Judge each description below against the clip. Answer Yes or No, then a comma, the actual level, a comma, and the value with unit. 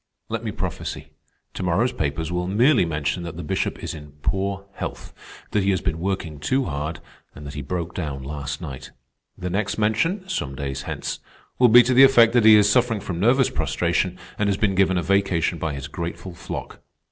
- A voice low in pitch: Yes, very low, 90 Hz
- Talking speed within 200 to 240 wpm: Yes, fast, 205 wpm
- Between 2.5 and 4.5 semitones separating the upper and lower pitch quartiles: No, average, 5.2 semitones